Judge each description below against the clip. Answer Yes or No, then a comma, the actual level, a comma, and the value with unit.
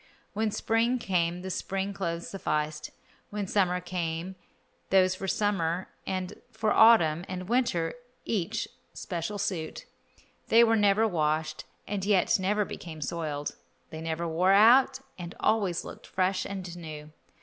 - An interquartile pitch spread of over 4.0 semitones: No, average, 3.7 semitones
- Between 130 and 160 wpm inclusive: Yes, average, 140 wpm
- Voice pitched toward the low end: No, medium, 185 Hz